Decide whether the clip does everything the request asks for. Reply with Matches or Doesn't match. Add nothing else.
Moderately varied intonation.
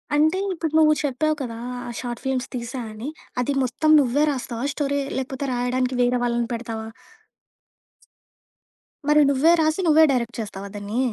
Matches